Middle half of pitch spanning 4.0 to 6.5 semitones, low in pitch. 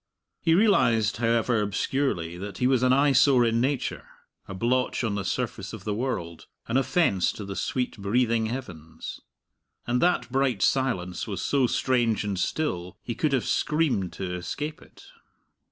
Yes: average, 5.0 semitones; low, 120 Hz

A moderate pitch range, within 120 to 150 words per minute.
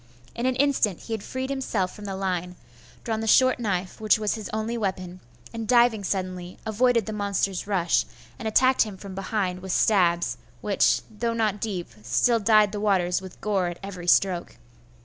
No: average, 3.4 semitones; average, 185 wpm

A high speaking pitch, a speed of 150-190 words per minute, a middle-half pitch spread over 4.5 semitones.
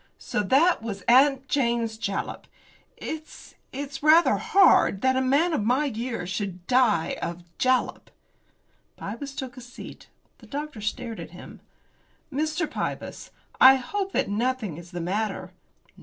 No: very high, 250 Hz; average, 140 wpm; average, 5.2 semitones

